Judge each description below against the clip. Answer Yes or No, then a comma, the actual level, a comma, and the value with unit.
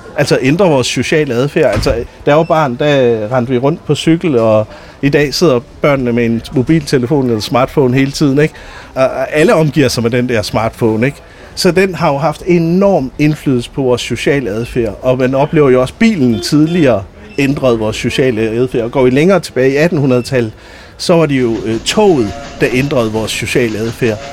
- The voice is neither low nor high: No, low, 130 Hz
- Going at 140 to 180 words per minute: No, average, 190 wpm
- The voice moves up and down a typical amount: Yes, average, 4.2 semitones